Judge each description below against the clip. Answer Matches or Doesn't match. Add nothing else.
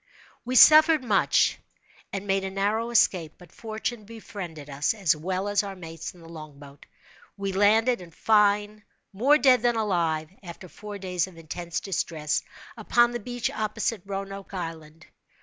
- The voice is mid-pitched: Doesn't match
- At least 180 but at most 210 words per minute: Doesn't match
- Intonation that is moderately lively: Matches